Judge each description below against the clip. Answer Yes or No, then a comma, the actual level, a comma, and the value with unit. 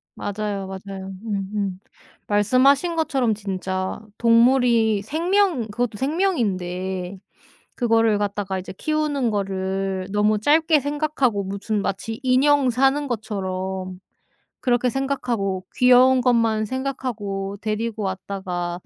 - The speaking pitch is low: No, high, 215 Hz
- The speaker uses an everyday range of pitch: Yes, average, 5.0 semitones